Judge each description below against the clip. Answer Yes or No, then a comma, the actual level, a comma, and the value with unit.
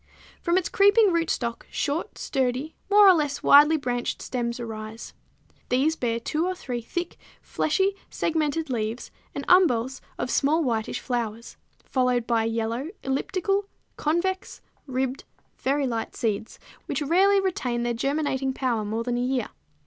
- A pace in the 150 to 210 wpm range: No, average, 140 wpm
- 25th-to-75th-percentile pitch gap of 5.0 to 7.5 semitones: Yes, wide, 5.6 semitones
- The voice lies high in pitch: Yes, very high, 265 Hz